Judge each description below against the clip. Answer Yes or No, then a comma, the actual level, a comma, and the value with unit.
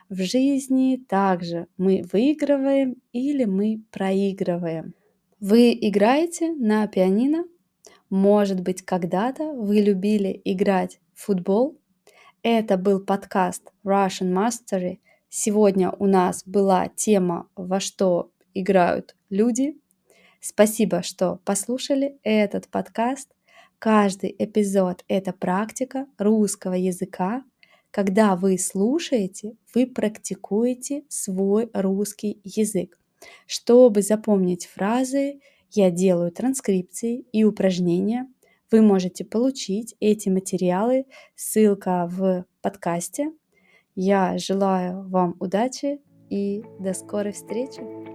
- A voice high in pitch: Yes, high, 200 Hz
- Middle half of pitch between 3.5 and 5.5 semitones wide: Yes, average, 3.8 semitones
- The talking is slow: Yes, slow, 95 wpm